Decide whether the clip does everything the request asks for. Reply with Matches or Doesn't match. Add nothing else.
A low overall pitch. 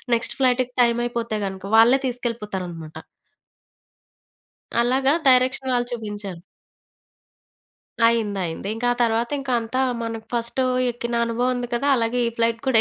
Doesn't match